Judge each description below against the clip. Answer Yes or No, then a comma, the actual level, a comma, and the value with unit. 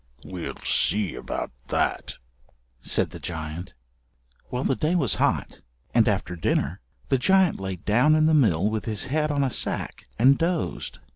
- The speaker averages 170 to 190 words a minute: No, average, 160 wpm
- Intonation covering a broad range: Yes, wide, 8.6 semitones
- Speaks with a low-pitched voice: Yes, low, 125 Hz